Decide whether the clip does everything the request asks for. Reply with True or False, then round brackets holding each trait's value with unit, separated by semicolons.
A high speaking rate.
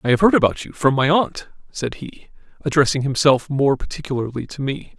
False (195 wpm)